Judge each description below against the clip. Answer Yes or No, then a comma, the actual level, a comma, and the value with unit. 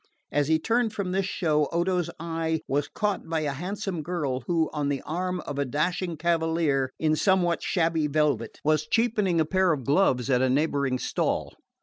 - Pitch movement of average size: Yes, average, 3.7 semitones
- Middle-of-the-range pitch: Yes, medium, 160 Hz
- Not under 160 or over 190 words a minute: Yes, average, 185 wpm